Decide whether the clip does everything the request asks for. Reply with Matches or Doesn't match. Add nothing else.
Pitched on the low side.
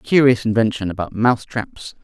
Matches